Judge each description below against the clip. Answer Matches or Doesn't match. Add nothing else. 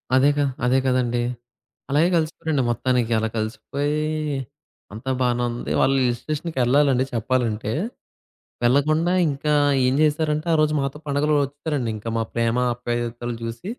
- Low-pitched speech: Matches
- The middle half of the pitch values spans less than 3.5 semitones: Doesn't match